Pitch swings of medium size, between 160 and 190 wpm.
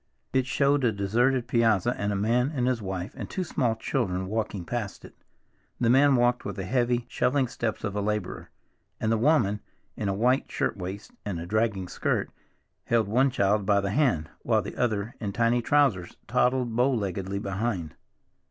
Yes: average, 3.8 semitones; average, 185 wpm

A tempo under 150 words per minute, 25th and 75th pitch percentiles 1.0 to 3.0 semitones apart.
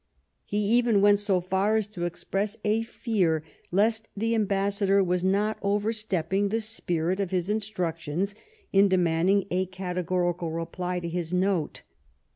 Yes: average, 140 wpm; average, 2.7 semitones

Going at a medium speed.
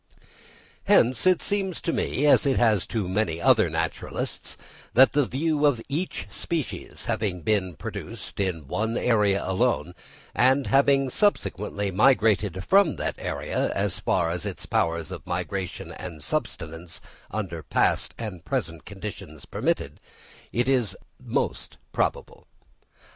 No: slow, 130 wpm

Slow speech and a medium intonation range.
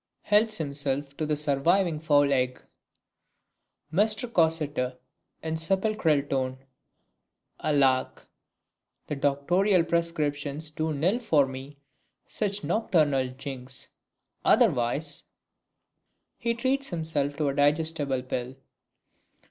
Yes: slow, 95 wpm; average, 3.5 semitones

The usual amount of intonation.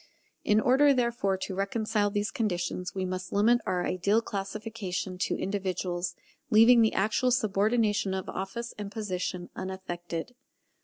Yes: average, 3.2 semitones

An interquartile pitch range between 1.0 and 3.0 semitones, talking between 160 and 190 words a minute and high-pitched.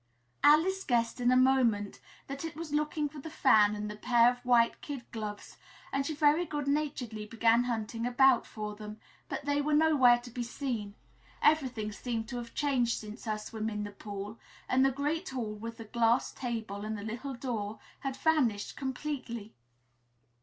No: average, 4.4 semitones; average, 180 wpm; high, 245 Hz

